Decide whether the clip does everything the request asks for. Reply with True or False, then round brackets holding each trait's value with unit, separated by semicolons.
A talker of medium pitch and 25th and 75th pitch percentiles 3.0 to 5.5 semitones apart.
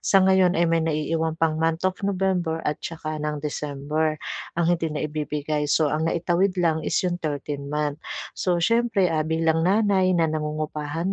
False (160 Hz; 2.6 semitones)